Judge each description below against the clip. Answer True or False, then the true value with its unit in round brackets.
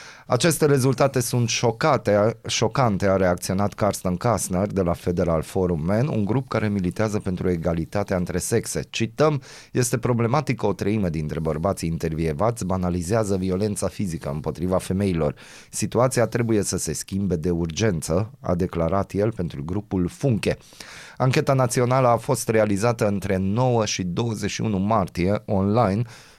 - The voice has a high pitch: False (100 Hz)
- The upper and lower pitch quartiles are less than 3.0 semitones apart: False (4.4 semitones)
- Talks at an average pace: True (135 wpm)